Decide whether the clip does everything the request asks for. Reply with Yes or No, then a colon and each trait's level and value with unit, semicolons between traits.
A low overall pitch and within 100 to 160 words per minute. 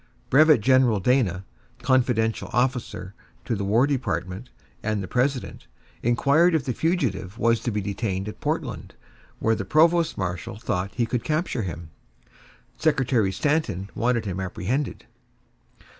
Yes: low, 115 Hz; slow, 135 wpm